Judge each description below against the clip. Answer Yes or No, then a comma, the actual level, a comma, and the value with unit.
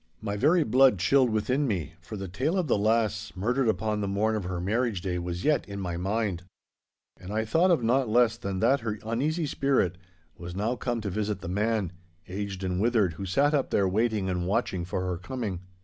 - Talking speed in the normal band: No, fast, 210 wpm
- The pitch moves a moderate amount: Yes, average, 4.5 semitones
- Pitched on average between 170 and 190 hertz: No, low, 105 Hz